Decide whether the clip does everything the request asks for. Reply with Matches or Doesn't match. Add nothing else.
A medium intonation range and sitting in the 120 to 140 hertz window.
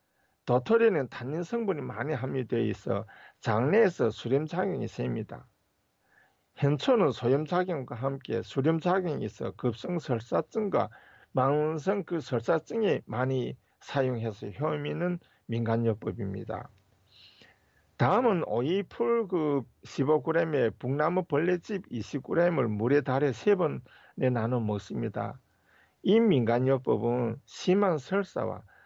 Doesn't match